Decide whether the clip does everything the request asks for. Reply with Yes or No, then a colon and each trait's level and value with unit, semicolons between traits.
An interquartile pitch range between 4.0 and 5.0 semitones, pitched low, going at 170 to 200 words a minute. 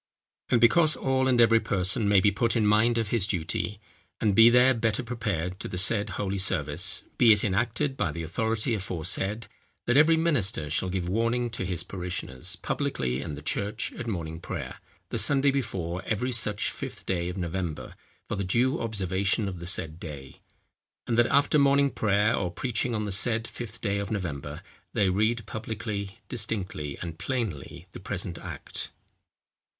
Yes: average, 4.5 semitones; low, 105 Hz; average, 175 wpm